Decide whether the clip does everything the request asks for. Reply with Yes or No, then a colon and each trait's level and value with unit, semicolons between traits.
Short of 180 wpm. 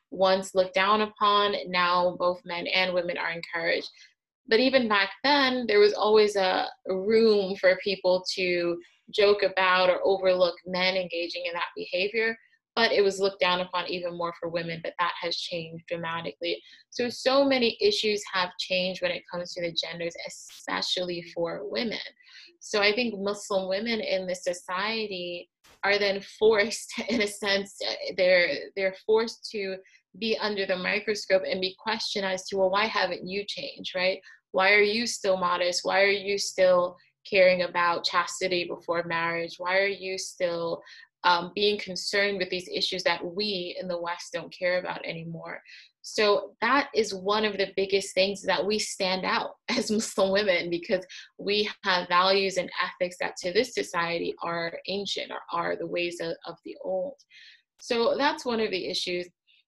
Yes: average, 170 wpm